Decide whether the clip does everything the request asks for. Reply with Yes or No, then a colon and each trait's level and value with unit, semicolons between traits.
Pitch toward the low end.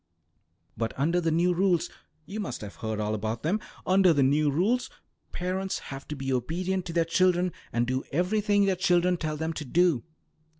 No: medium, 170 Hz